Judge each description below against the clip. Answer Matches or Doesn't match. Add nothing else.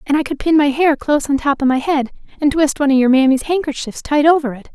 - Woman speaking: Matches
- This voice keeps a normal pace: Doesn't match